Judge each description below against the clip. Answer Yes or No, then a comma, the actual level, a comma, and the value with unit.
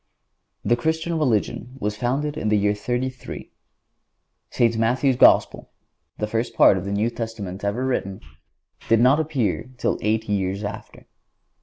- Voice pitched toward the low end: Yes, low, 115 Hz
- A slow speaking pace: No, average, 145 wpm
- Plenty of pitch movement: No, average, 3.8 semitones